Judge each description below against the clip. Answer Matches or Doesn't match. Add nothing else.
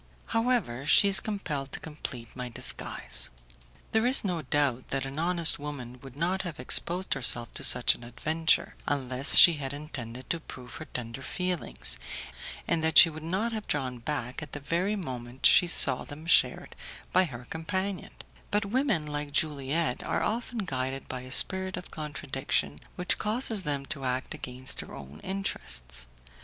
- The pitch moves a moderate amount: Doesn't match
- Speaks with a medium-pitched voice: Matches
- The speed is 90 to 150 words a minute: Doesn't match